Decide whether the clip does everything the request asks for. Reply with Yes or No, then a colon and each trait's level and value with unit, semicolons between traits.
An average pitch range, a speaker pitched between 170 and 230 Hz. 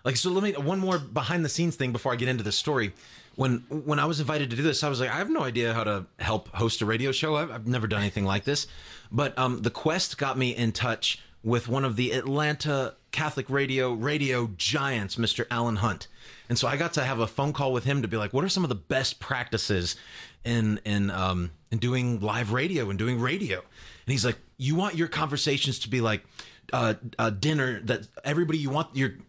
No: average, 4.3 semitones; low, 130 Hz